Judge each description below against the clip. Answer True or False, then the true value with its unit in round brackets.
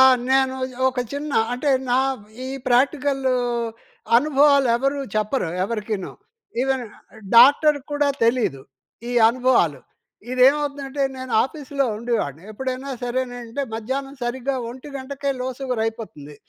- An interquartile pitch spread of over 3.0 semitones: False (2.7 semitones)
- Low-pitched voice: False (260 Hz)